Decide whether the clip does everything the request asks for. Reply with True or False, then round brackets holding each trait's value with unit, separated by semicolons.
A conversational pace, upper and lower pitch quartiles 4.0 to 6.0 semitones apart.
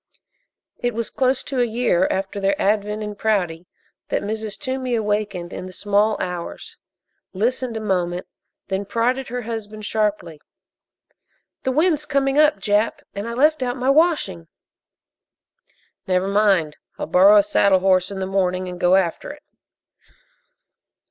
True (150 wpm; 4.5 semitones)